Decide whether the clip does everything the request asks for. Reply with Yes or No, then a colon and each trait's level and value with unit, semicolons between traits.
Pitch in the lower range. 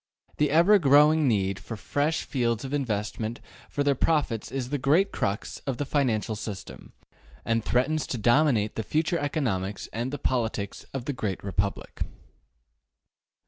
Yes: low, 125 Hz